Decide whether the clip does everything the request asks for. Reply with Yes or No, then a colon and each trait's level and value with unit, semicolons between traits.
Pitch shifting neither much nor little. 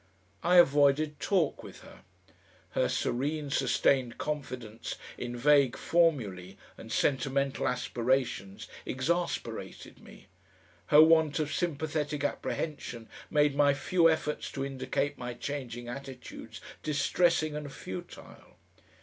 Yes: average, 3.4 semitones